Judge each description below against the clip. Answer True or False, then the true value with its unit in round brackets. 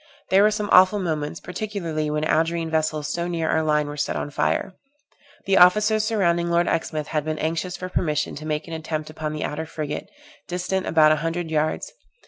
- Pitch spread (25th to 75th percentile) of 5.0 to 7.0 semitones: False (2.8 semitones)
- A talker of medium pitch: True (160 Hz)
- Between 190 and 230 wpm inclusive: True (195 wpm)